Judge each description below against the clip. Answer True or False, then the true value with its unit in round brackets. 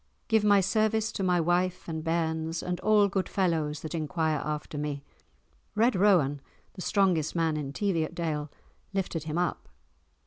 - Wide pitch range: False (3.7 semitones)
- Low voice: False (170 Hz)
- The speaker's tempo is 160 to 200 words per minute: False (150 wpm)